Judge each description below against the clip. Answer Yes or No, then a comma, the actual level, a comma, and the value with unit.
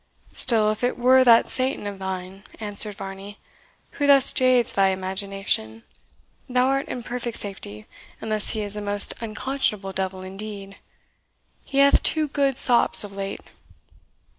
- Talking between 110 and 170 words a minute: Yes, average, 150 wpm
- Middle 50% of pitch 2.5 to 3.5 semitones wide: No, average, 4.3 semitones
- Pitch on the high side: Yes, high, 210 Hz